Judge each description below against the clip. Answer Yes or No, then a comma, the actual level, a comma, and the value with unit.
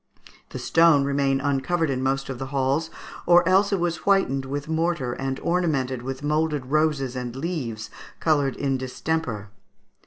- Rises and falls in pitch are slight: No, average, 3.5 semitones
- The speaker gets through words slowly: No, average, 155 wpm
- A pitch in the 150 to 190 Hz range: No, medium, 140 Hz